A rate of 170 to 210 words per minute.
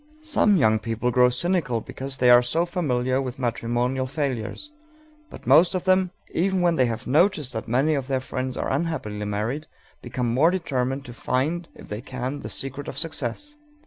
Yes: average, 180 wpm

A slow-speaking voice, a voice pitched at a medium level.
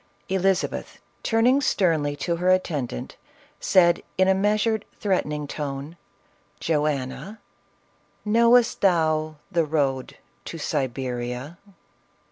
Yes: slow, 95 wpm; medium, 165 Hz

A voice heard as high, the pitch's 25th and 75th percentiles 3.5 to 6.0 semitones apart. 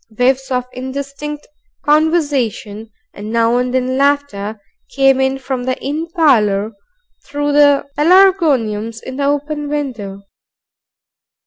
Yes: very high, 270 Hz; average, 4.0 semitones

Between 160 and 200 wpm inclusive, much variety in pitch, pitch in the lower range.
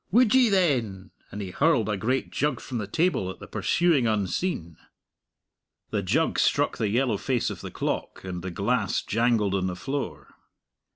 Yes: average, 175 wpm; wide, 6.9 semitones; low, 115 Hz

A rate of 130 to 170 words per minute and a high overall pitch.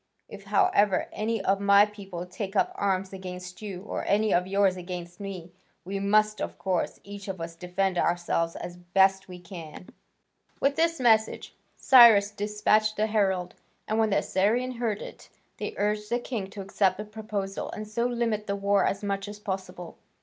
No: average, 180 wpm; high, 200 Hz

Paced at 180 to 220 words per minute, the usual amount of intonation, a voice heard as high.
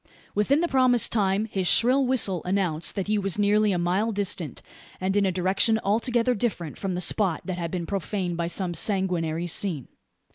Yes: average, 185 wpm; average, 3.3 semitones; high, 195 Hz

